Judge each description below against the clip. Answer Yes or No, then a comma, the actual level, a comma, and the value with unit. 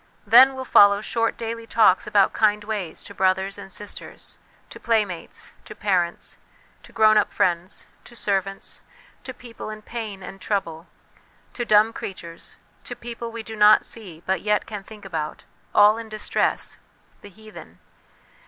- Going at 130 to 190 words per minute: Yes, average, 155 wpm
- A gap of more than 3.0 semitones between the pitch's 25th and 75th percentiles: No, average, 2.7 semitones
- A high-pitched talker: Yes, high, 210 Hz